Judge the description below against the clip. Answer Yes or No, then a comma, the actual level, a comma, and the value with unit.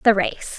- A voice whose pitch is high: Yes, high, 210 Hz